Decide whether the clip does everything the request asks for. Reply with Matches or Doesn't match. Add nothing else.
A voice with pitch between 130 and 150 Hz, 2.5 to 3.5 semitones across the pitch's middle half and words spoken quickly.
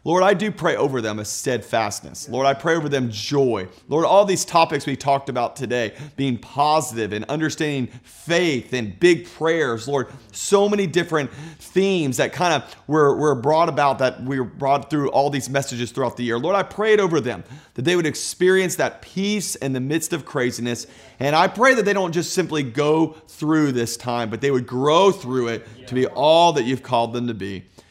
Doesn't match